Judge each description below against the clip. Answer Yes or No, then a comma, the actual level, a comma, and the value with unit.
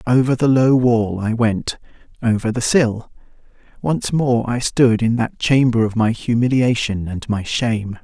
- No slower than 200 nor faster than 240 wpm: No, average, 155 wpm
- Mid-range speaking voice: No, low, 115 Hz